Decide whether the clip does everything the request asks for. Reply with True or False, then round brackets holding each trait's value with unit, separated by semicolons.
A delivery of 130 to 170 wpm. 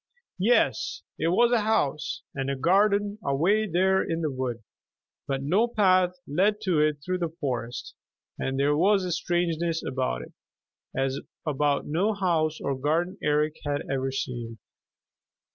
True (150 wpm)